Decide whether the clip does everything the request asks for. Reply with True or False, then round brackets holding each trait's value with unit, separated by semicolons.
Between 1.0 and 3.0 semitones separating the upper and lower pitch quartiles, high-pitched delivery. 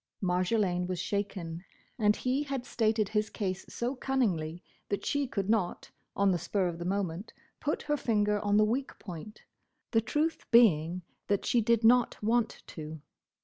False (4.4 semitones; 210 Hz)